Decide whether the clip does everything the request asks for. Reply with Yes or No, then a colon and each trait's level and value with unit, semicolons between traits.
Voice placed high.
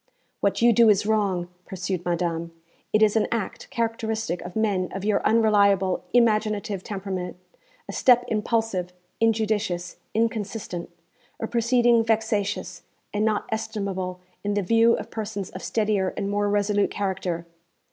Yes: high, 205 Hz